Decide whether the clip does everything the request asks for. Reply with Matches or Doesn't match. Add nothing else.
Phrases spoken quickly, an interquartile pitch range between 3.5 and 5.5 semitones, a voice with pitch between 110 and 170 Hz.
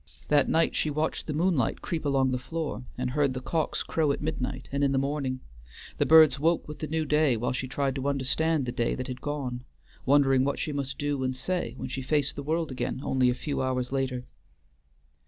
Doesn't match